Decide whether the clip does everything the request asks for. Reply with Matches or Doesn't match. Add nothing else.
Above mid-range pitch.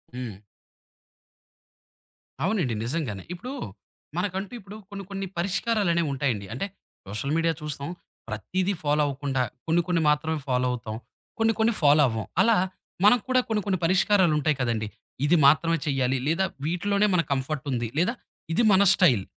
Doesn't match